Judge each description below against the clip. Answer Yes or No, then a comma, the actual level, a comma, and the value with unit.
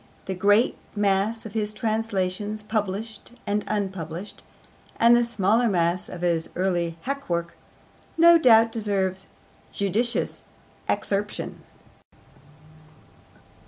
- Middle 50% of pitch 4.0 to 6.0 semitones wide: No, average, 3.1 semitones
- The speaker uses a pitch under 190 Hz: No, high, 205 Hz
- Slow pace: Yes, slow, 95 wpm